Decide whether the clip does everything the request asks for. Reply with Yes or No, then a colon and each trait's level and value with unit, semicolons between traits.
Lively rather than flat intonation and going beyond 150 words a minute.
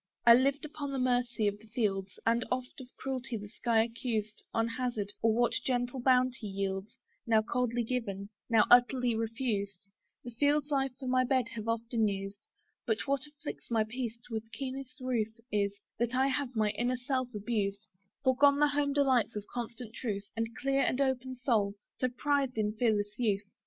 No: average, 3.1 semitones; average, 175 wpm